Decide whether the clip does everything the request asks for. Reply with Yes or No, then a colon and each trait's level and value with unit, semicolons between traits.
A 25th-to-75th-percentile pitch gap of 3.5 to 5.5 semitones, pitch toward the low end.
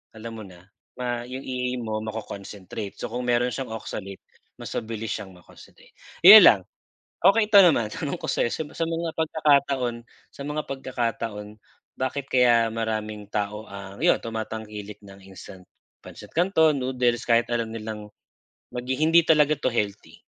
Yes: average, 4.0 semitones; low, 115 Hz